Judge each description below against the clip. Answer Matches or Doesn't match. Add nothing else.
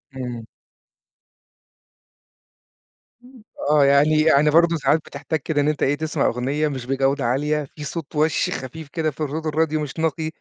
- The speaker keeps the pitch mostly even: Matches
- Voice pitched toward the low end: Doesn't match